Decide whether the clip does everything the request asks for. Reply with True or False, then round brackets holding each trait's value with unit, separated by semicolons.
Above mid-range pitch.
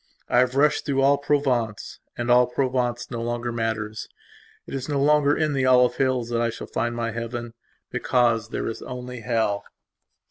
False (120 Hz)